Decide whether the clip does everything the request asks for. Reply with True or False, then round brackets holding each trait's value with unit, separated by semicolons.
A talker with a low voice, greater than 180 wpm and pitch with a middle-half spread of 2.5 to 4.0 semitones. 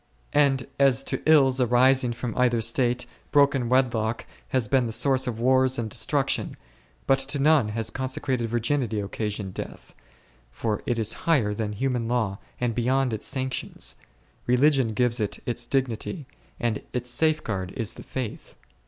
False (125 Hz; 155 wpm; 2.9 semitones)